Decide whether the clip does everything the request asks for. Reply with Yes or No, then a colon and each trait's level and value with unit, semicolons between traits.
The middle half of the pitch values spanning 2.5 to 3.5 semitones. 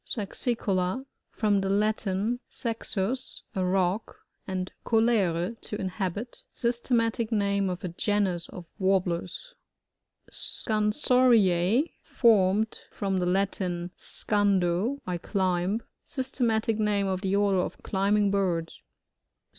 Yes: average, 3.2 semitones